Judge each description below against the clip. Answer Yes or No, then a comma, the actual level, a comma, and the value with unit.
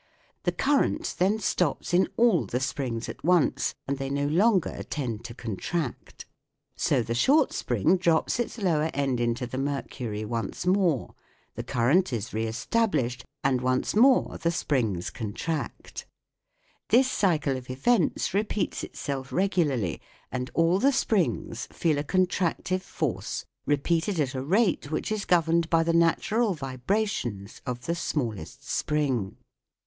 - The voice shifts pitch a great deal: Yes, wide, 6.7 semitones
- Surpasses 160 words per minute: No, average, 145 wpm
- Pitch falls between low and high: Yes, medium, 150 Hz